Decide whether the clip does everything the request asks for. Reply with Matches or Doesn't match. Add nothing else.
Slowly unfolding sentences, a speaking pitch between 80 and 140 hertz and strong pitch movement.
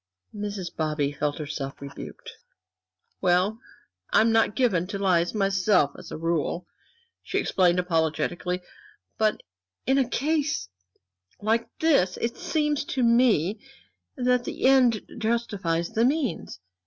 Doesn't match